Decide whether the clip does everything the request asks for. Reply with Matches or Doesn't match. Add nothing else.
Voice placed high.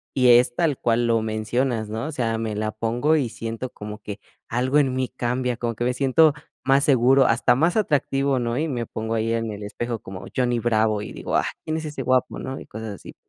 Doesn't match